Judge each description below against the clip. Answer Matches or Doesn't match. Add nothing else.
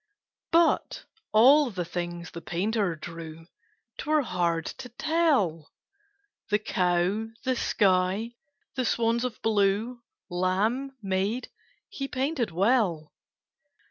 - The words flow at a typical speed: Doesn't match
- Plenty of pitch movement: Matches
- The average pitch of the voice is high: Matches